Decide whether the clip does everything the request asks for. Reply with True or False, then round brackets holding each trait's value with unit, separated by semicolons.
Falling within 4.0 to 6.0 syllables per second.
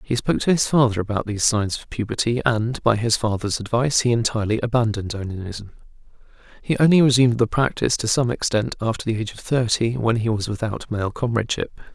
False (6.4 syllables/s)